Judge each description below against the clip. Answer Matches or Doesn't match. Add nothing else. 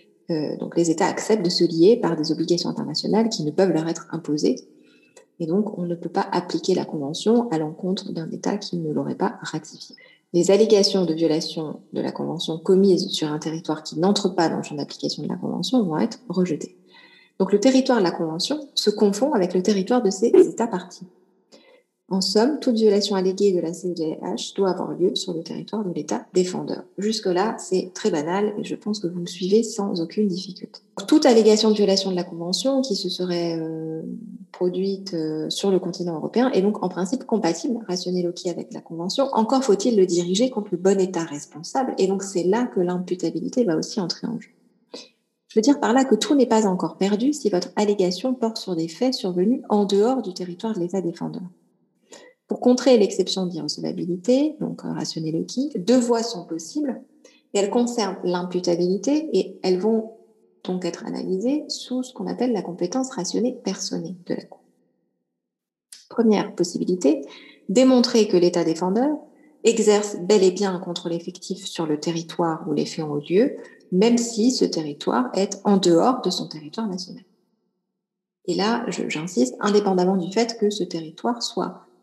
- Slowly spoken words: Doesn't match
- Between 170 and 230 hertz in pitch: Matches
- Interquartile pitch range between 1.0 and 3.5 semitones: Doesn't match